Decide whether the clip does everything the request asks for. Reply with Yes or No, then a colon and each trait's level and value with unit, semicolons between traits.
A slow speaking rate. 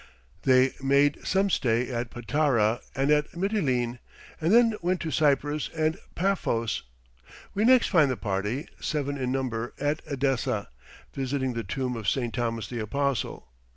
No: average, 150 wpm